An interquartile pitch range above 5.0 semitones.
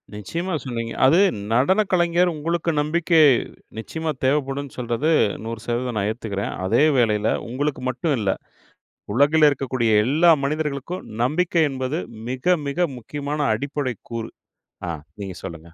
Yes: wide, 5.4 semitones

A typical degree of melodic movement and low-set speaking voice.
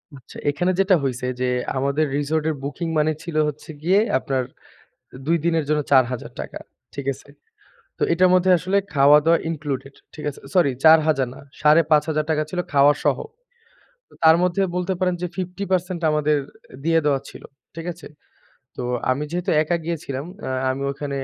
No: average, 3.4 semitones; medium, 155 Hz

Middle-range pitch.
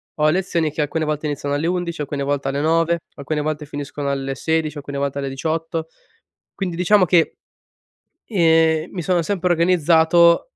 Yes: medium, 160 Hz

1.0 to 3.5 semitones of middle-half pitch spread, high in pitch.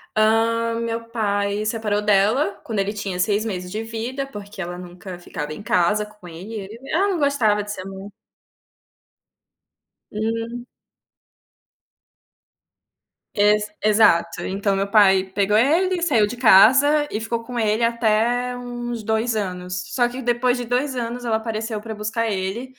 Yes: average, 2.9 semitones; high, 220 Hz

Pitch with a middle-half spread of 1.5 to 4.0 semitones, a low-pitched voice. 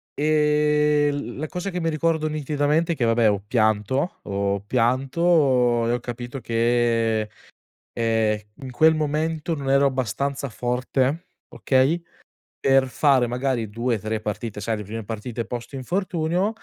No: average, 4.6 semitones; low, 130 Hz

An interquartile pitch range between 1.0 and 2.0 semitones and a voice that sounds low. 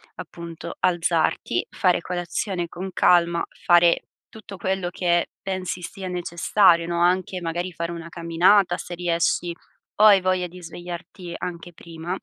No: narrow, 1.4 semitones; medium, 175 Hz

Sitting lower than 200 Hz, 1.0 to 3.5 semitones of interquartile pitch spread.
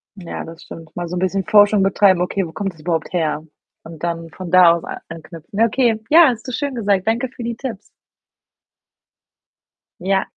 No: medium, 185 Hz; average, 4.7 semitones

